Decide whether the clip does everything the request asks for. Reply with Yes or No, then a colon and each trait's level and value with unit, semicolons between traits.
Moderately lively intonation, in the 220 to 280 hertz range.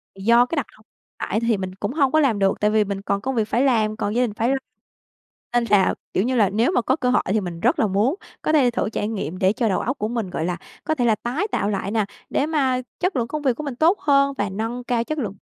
Yes: average, 4.4 semitones; high, 230 Hz